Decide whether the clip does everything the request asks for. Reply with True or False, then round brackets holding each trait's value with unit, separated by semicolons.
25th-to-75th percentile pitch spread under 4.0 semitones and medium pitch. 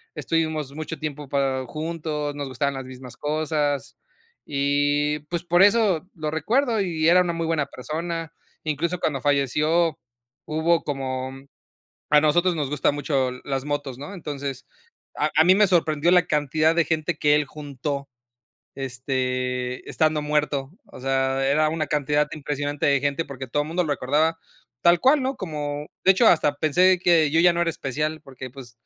True (2.8 semitones; 150 Hz)